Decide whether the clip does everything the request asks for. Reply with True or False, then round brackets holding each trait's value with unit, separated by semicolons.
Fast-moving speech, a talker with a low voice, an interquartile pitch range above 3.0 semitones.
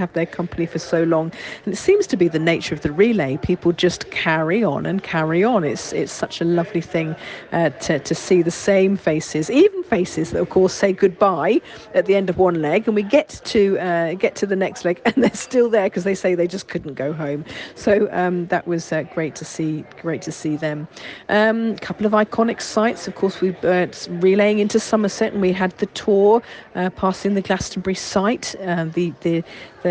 False (225 wpm; 185 Hz; 3.5 semitones)